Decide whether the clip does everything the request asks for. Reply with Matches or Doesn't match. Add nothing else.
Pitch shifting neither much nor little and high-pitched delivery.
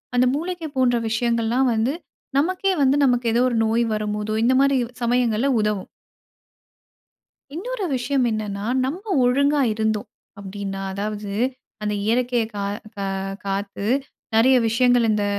Matches